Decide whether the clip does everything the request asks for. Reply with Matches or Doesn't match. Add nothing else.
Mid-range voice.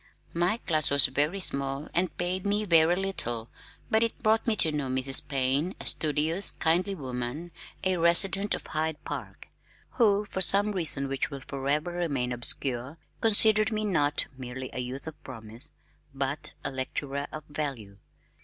Matches